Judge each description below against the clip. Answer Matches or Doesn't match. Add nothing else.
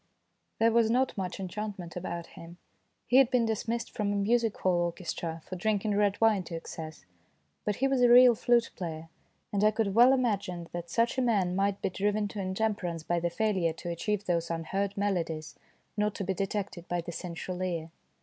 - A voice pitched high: Matches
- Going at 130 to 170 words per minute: Doesn't match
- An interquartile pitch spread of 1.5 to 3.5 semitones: Doesn't match